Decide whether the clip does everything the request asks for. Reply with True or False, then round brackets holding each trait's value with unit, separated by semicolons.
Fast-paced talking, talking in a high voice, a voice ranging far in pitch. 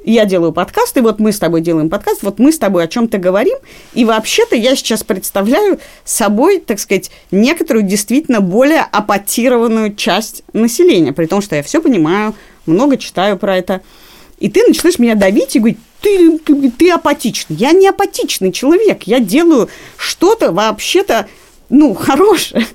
True (165 wpm; 230 Hz; 7.5 semitones)